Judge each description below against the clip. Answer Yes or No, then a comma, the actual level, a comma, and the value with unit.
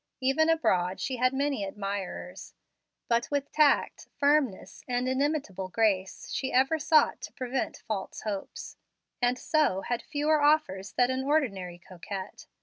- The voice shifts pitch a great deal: Yes, wide, 6.6 semitones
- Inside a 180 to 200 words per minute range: No, average, 140 wpm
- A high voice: Yes, very high, 255 Hz